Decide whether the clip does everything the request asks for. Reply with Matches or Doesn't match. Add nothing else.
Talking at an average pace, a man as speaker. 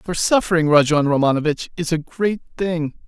Matches